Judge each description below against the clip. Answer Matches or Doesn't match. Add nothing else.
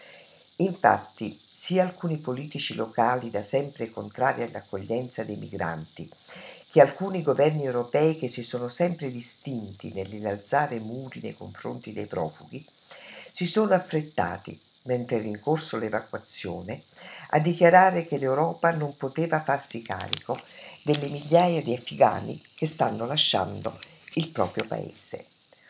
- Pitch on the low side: Matches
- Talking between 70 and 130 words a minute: Matches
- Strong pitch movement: Matches